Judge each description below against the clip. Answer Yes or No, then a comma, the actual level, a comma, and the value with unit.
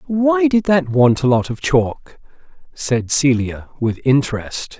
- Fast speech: No, average, 150 wpm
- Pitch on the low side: No, medium, 145 Hz